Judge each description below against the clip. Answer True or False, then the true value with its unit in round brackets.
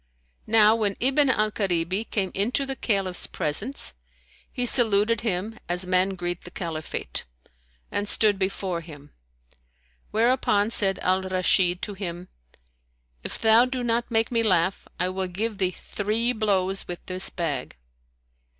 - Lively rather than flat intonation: False (3.6 semitones)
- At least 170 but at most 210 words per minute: False (140 wpm)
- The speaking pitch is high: True (195 Hz)